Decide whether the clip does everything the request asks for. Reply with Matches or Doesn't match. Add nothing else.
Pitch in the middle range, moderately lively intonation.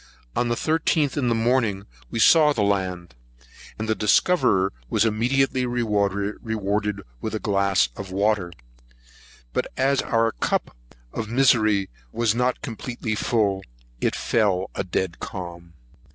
Doesn't match